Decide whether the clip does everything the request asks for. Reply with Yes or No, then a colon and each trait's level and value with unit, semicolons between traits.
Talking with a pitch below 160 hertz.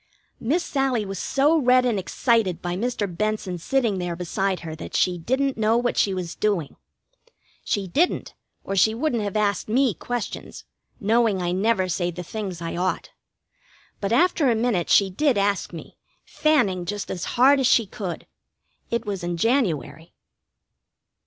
No: high, 205 Hz